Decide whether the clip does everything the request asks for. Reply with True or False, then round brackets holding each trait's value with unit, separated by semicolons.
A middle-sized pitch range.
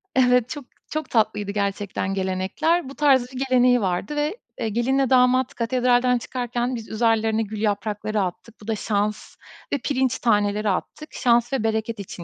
True (3.5 semitones)